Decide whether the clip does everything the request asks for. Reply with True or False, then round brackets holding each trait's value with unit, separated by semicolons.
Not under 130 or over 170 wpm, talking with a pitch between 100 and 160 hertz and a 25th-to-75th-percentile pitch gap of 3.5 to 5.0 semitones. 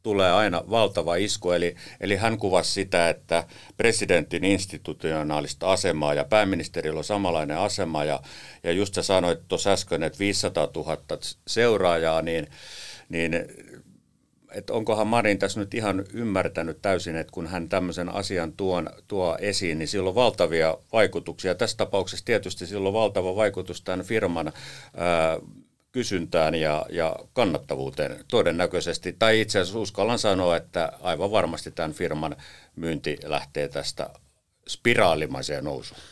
False (135 wpm; 90 Hz; 3.8 semitones)